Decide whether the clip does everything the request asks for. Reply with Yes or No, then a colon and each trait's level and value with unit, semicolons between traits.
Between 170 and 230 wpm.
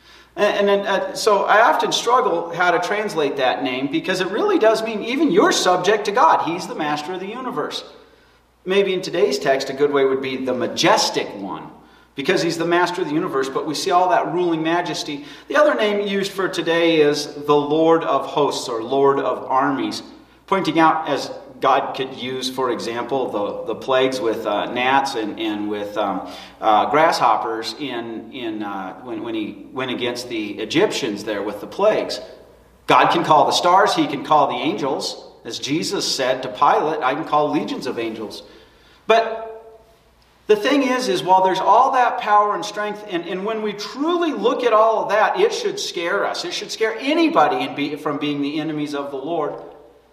Yes: average, 195 wpm